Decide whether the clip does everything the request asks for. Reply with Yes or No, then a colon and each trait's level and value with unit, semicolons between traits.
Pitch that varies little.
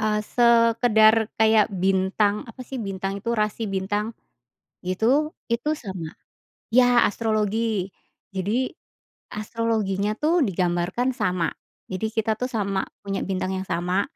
No: average, 3.2 semitones